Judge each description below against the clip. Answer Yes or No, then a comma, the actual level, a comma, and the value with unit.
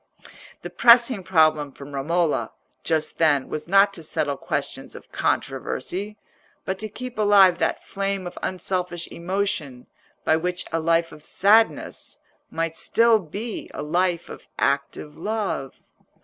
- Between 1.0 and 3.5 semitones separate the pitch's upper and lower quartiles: No, average, 4.3 semitones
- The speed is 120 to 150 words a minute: Yes, slow, 135 wpm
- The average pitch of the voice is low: No, medium, 175 Hz